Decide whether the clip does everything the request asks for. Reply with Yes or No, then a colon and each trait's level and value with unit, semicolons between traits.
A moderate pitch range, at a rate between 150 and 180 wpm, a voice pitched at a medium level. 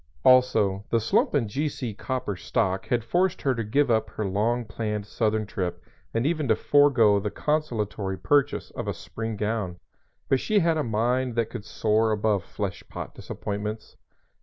No: average, 3.5 semitones; average, 170 wpm; low, 110 Hz